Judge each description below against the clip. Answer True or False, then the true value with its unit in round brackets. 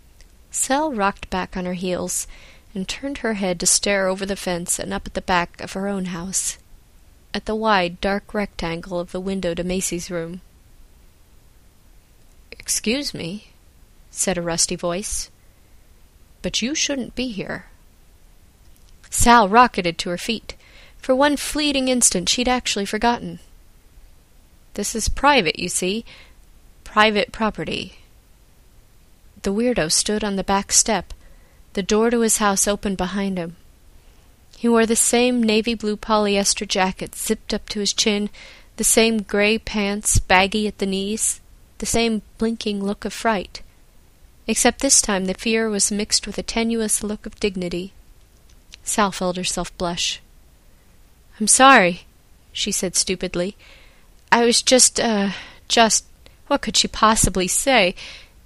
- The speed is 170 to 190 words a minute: False (145 wpm)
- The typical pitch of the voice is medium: False (200 Hz)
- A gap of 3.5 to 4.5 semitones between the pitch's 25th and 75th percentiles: True (3.9 semitones)